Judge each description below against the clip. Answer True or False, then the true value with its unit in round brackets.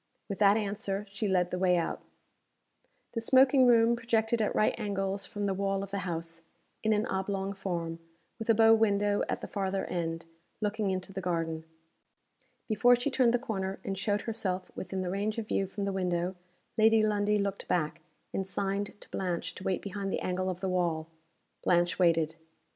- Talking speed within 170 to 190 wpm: True (185 wpm)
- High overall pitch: True (195 Hz)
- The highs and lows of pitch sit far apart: False (2.7 semitones)